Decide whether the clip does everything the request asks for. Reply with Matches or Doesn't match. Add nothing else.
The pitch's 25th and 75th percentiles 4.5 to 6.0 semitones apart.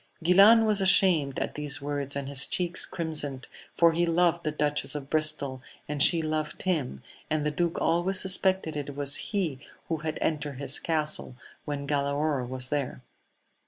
Doesn't match